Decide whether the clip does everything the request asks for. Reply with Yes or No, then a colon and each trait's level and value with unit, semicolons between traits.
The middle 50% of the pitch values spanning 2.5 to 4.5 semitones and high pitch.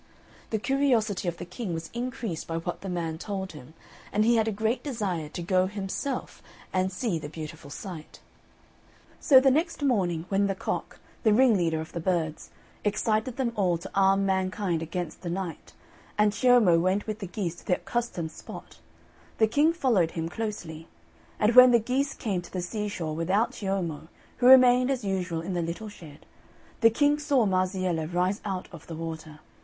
No: average, 5.0 semitones; high, 195 Hz